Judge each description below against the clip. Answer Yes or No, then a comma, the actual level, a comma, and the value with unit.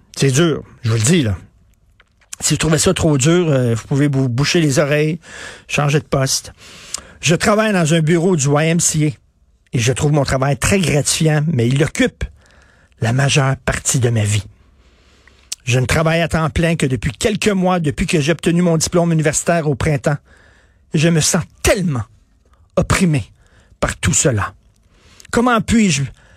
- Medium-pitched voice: Yes, medium, 145 Hz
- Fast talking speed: No, average, 170 wpm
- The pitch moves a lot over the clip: Yes, wide, 7.6 semitones